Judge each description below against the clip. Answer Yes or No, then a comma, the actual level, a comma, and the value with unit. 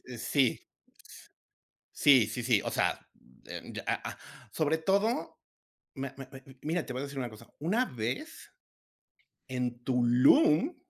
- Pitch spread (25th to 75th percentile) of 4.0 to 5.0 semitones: Yes, average, 4.5 semitones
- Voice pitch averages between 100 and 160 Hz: Yes, low, 135 Hz